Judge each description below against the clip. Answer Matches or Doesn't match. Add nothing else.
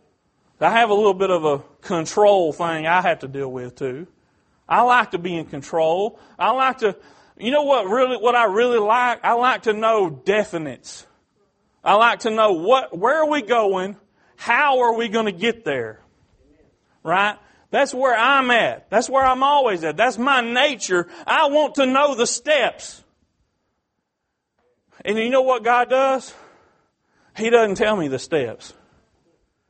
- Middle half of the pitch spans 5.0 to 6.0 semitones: Matches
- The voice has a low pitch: Doesn't match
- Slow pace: Doesn't match